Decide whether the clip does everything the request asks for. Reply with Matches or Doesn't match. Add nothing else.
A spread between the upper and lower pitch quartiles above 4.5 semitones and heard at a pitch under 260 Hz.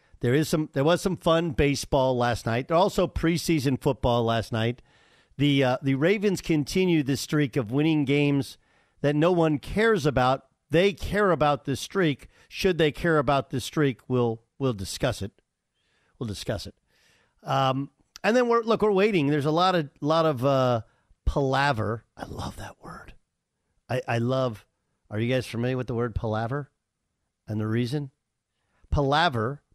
Matches